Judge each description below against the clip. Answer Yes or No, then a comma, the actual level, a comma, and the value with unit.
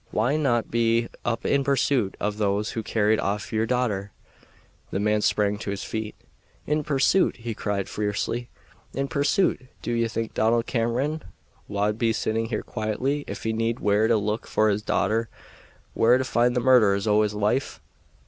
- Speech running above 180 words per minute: No, average, 175 wpm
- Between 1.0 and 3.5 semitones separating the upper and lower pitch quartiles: Yes, average, 2.7 semitones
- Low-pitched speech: Yes, low, 115 Hz